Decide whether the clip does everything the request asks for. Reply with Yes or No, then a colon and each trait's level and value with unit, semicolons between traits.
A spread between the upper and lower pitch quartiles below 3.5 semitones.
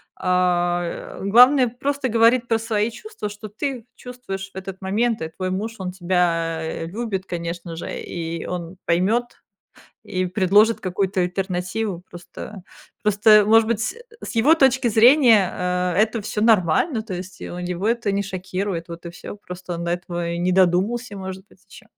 No: average, 3.9 semitones